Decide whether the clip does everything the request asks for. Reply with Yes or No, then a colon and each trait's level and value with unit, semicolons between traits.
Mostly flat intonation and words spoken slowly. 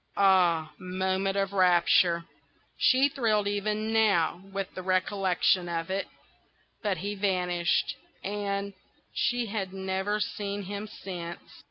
Yes: narrow, 2.0 semitones; slow, 115 wpm